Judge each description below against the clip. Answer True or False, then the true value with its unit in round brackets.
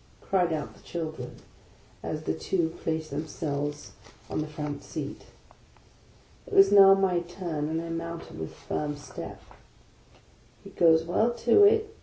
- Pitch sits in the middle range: True (165 Hz)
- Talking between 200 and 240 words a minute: False (160 wpm)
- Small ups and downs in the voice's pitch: False (4.2 semitones)